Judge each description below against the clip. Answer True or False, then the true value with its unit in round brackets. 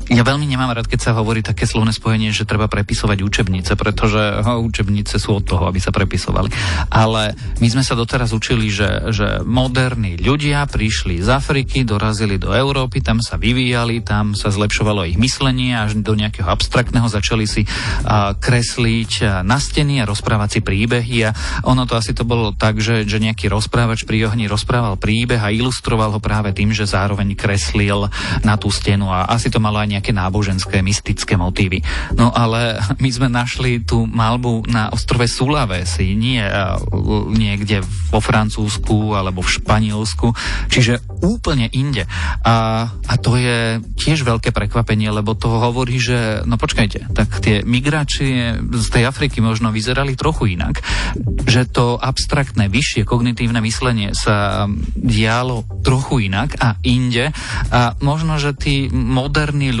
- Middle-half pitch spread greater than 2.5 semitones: True (2.9 semitones)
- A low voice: True (110 Hz)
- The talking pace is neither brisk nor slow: True (155 wpm)